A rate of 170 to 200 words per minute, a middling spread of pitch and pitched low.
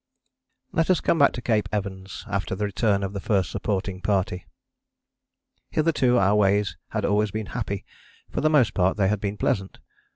No: average, 175 wpm; narrow, 2.2 semitones; low, 100 Hz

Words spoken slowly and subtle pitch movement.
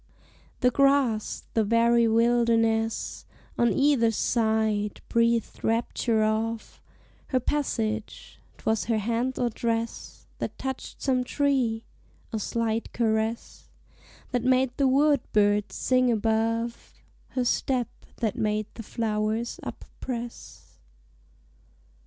Yes: slow, 110 wpm; narrow, 2.2 semitones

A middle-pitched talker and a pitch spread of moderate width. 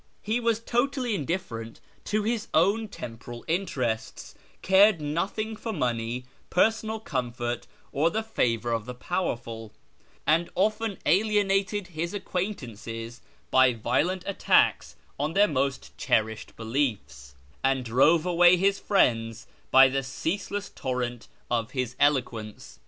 No: medium, 145 Hz; wide, 8.8 semitones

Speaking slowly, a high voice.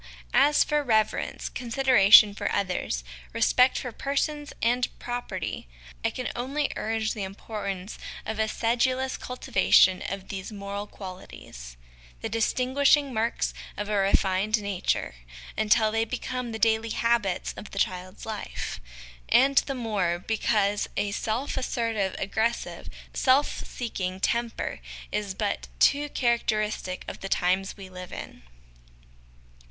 Yes: slow, 130 wpm; high, 220 Hz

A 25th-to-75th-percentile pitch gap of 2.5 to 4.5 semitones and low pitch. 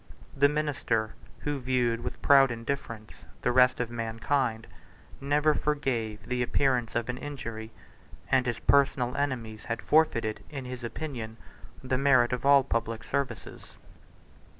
Yes: average, 3.2 semitones; low, 125 Hz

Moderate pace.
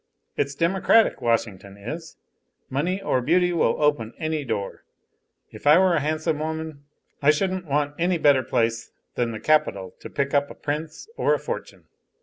Yes: average, 165 wpm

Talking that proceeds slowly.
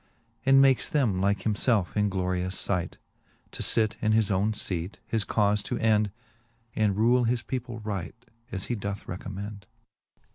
No: average, 155 wpm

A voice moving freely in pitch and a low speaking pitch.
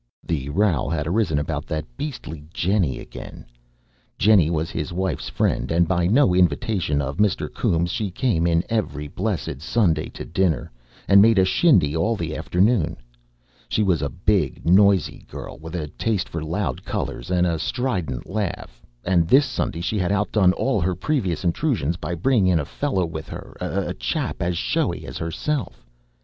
No: average, 4.4 semitones; very low, 90 Hz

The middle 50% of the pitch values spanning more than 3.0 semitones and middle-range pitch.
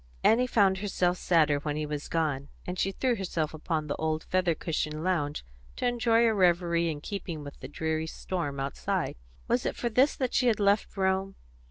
Yes: average, 4.8 semitones; medium, 175 Hz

